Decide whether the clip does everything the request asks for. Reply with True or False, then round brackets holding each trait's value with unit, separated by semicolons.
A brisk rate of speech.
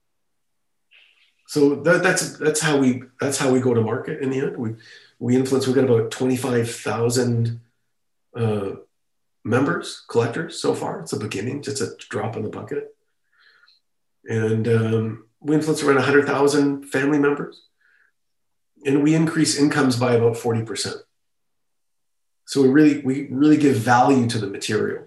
False (160 wpm)